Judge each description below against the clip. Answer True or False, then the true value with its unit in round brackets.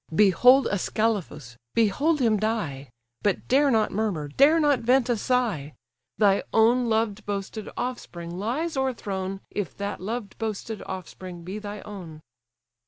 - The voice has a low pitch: False (215 Hz)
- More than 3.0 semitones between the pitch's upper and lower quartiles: True (4.3 semitones)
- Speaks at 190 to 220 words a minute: False (135 wpm)